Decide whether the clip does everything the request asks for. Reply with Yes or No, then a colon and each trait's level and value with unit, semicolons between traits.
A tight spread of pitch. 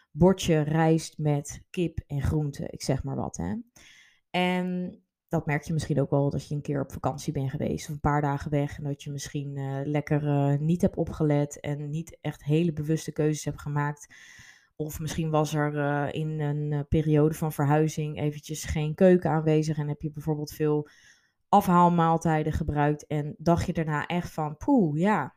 Yes: narrow, 1.8 semitones